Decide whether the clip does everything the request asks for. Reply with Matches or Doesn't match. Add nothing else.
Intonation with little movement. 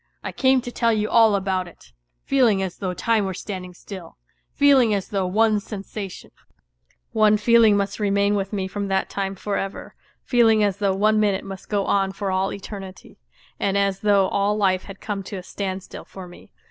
Matches